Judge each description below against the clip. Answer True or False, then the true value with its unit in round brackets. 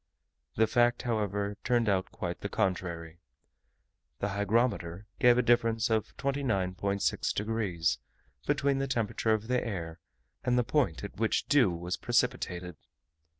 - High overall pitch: False (105 Hz)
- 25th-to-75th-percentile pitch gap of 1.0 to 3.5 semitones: False (4.6 semitones)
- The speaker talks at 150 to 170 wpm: False (135 wpm)